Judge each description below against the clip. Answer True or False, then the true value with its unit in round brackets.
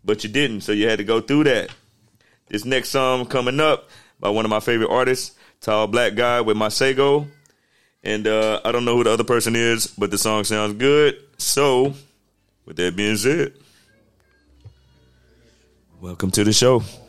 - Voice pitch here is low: True (110 Hz)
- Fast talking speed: False (180 wpm)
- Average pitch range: True (3.5 semitones)